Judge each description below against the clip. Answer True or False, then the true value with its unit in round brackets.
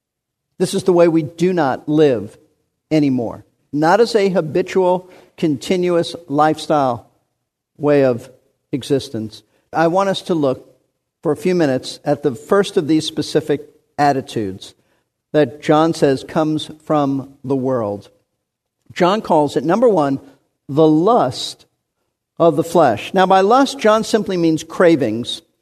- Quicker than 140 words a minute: False (135 wpm)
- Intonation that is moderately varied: True (4.1 semitones)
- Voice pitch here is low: False (155 Hz)